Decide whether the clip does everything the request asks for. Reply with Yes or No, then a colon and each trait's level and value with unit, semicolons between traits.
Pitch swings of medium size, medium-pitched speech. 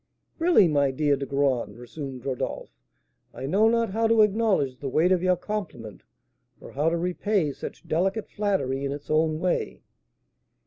No: wide, 6.6 semitones; medium, 160 Hz